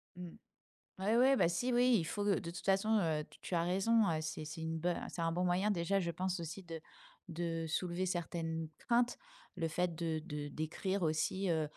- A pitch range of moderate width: Yes, average, 3.1 semitones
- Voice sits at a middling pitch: Yes, medium, 175 Hz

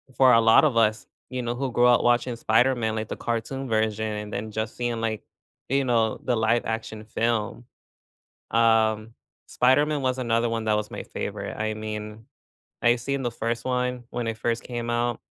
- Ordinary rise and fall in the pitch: No, narrow, 1.9 semitones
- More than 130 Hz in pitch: No, low, 115 Hz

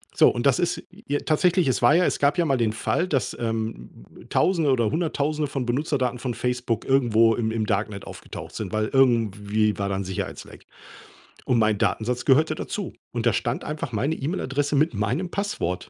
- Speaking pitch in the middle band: No, low, 125 Hz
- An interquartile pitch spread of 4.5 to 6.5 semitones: Yes, average, 5.2 semitones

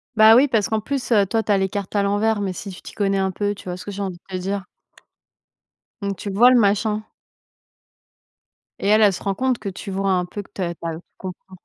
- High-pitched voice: Yes, high, 200 Hz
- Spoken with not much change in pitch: Yes, narrow, 2.1 semitones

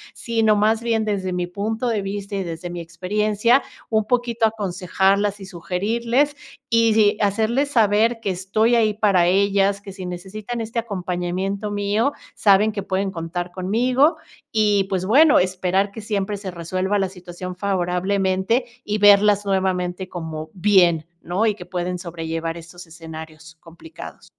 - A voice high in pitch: Yes, high, 200 Hz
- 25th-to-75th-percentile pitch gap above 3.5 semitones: No, average, 3.1 semitones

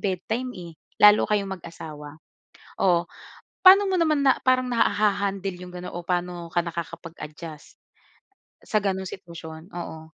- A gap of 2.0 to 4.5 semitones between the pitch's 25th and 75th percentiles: Yes, average, 3.7 semitones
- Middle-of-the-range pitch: Yes, medium, 180 Hz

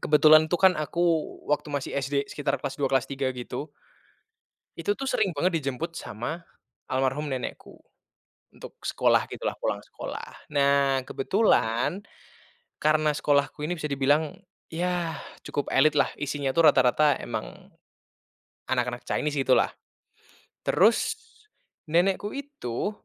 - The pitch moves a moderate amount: Yes, average, 3.8 semitones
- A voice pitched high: No, medium, 145 Hz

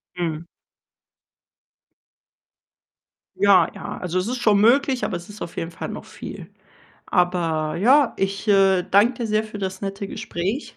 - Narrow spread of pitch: No, average, 3.4 semitones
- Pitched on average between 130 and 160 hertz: No, high, 195 Hz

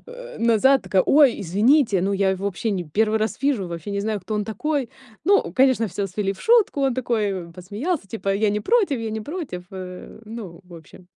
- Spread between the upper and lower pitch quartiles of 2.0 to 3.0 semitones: No, wide, 5.6 semitones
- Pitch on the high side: Yes, high, 215 Hz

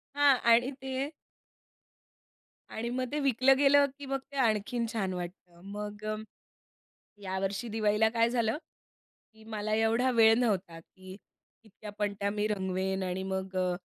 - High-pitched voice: Yes, high, 215 Hz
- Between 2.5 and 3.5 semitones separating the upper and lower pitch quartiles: No, average, 4.2 semitones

